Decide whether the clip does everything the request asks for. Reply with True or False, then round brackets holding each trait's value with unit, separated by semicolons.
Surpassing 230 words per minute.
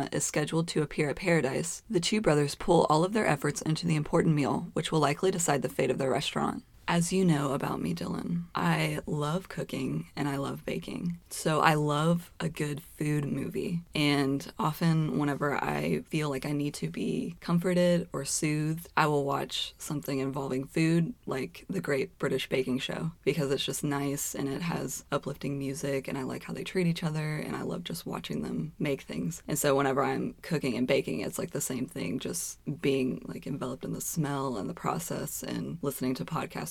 False (200 wpm)